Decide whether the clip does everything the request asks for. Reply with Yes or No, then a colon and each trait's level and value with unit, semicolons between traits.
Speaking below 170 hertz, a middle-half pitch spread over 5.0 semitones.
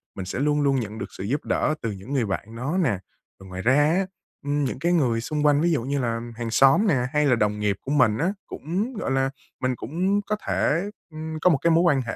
Yes: medium, 140 Hz; wide, 5.6 semitones